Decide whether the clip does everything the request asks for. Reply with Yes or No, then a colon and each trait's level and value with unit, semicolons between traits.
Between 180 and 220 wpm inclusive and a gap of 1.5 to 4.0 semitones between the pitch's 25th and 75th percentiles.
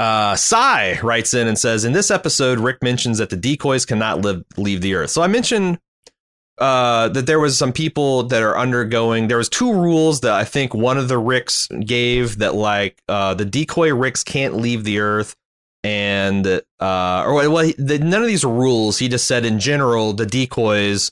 No: average, 200 wpm; average, 4.7 semitones